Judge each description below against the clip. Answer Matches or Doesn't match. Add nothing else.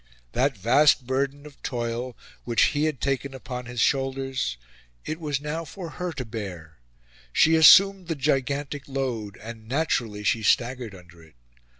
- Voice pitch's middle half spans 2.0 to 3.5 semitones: Doesn't match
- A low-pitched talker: Matches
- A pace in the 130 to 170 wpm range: Matches